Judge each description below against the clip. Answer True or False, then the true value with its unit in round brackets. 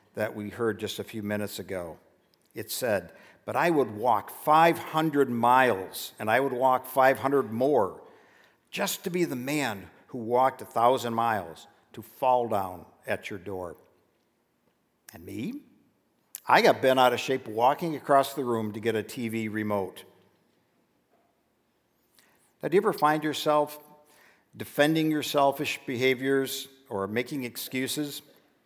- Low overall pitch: True (130 Hz)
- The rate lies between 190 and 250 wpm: False (140 wpm)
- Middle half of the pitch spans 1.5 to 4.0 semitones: False (4.5 semitones)